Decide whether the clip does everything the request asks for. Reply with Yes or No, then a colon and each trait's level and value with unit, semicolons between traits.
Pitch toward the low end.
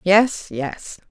No: high, 190 Hz